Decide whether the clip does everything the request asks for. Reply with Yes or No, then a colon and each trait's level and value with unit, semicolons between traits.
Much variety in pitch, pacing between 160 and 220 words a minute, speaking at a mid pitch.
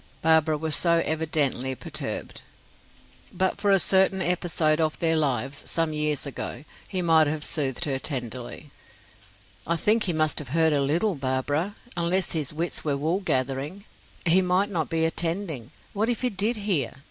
No: average, 3.8 semitones; average, 165 wpm; medium, 160 Hz